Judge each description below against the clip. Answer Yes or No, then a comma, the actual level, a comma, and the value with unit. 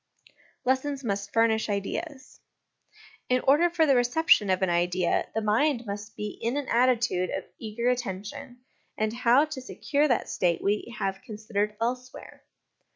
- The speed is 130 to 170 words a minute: Yes, average, 150 wpm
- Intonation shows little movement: No, average, 4.1 semitones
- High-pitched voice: Yes, high, 235 Hz